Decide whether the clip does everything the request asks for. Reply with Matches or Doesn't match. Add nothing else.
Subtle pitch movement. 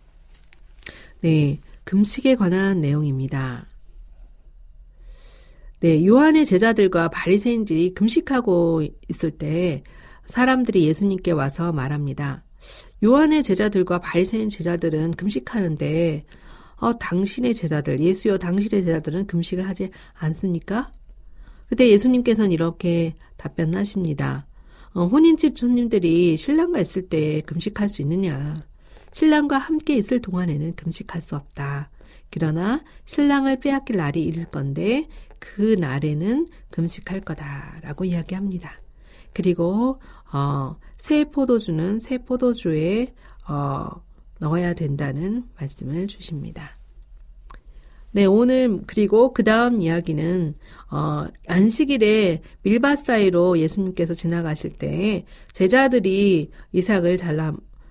Doesn't match